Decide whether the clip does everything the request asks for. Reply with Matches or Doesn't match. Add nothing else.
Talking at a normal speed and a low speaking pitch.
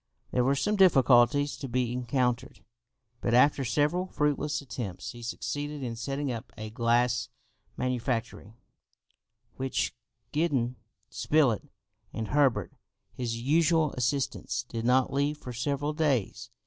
Doesn't match